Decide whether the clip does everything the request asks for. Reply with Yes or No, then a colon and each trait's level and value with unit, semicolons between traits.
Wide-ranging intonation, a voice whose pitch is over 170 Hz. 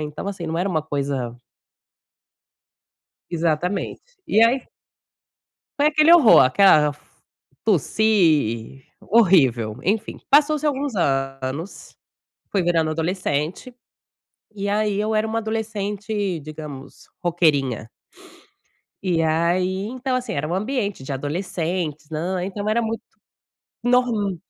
Yes: wide, 6.1 semitones; medium, 185 Hz